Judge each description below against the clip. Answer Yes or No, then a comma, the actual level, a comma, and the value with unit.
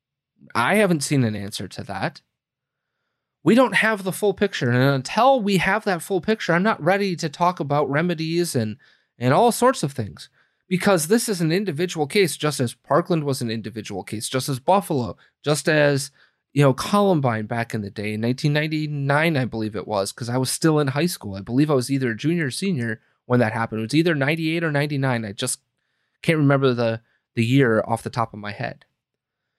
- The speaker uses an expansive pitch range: Yes, wide, 6.4 semitones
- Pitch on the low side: No, medium, 145 Hz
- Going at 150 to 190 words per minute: No, fast, 205 wpm